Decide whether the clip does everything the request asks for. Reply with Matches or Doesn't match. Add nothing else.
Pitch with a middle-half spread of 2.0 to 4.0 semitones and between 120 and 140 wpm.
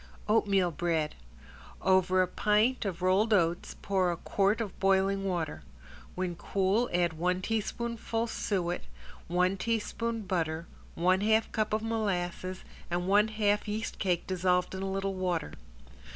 Matches